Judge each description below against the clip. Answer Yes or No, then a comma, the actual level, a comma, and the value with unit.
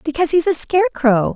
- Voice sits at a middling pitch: No, very high, 300 Hz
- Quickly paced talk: No, average, 175 wpm